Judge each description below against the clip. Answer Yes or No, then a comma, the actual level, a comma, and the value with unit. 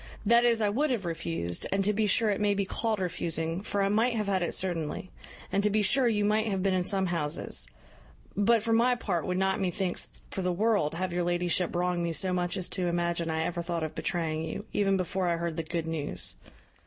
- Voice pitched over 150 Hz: Yes, medium, 185 Hz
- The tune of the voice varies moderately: Yes, average, 3.3 semitones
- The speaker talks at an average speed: No, fast, 235 wpm